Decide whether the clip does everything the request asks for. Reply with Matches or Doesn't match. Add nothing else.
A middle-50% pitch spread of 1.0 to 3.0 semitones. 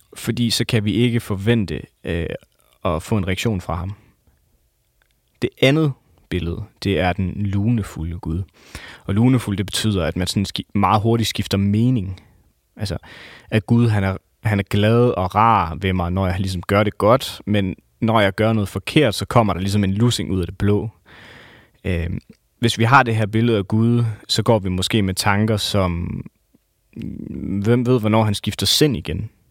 Doesn't match